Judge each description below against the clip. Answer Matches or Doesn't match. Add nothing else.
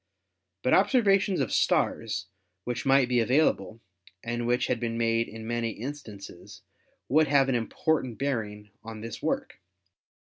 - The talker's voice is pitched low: Matches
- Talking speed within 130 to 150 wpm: Matches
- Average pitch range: Matches